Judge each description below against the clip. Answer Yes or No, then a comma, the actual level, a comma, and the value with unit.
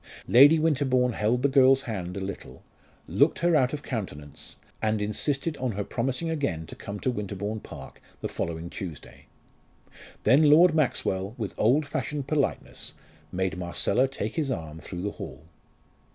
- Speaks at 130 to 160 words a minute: Yes, average, 155 wpm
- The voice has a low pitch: Yes, low, 120 Hz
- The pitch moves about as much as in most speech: No, wide, 6.8 semitones